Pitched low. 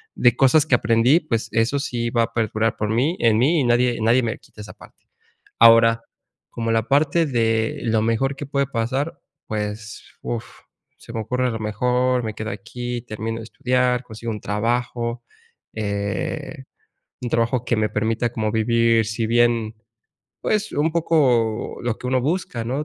Yes: low, 115 Hz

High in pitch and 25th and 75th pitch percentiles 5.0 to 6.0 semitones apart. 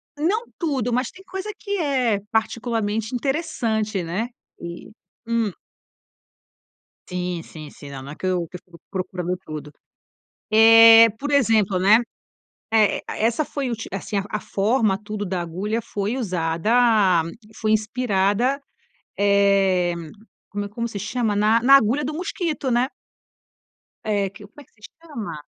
No: high, 215 Hz; average, 4.4 semitones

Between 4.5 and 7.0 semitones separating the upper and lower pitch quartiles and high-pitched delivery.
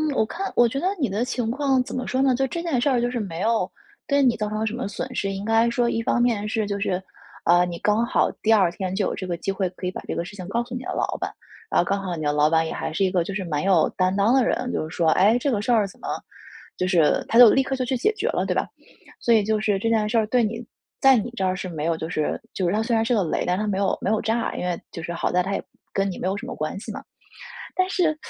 Yes: average, 4.8 semitones; high, 210 Hz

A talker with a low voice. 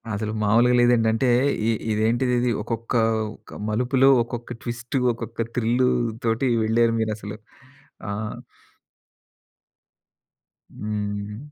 Yes: low, 115 Hz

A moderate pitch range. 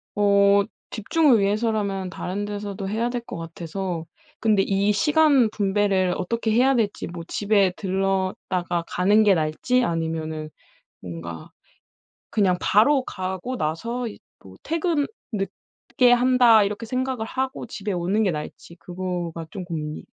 Yes: average, 4.4 semitones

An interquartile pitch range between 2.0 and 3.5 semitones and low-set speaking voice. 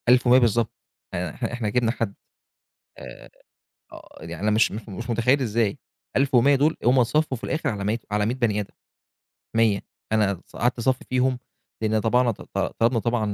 Yes: average, 2.9 semitones; low, 115 Hz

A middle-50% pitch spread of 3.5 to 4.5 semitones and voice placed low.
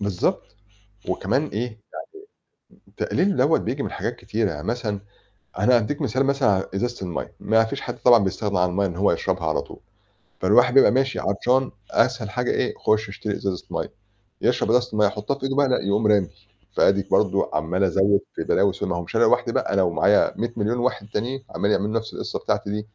Yes: average, 3.9 semitones; low, 105 Hz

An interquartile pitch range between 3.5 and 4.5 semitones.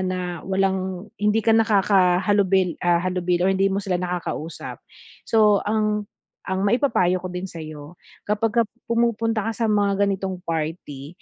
No: average, 2.8 semitones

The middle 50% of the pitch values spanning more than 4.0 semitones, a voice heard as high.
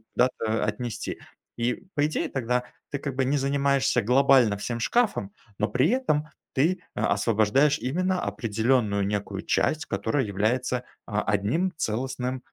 No: average, 4.7 semitones; low, 125 Hz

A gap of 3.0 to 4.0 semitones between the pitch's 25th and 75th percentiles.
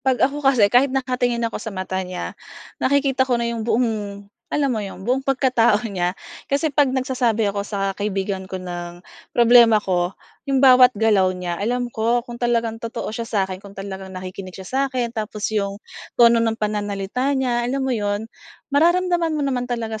No: average, 4.4 semitones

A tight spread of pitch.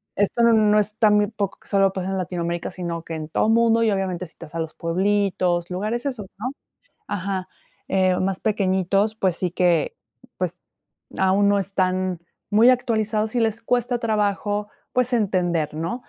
No: average, 3.1 semitones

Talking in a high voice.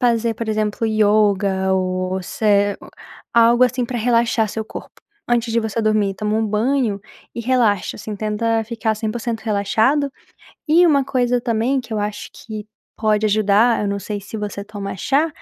Yes: high, 220 Hz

